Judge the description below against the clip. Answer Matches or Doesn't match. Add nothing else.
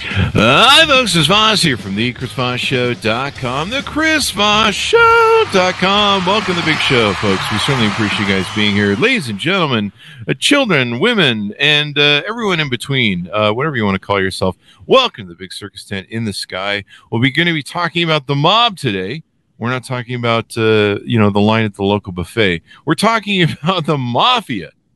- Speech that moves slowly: Doesn't match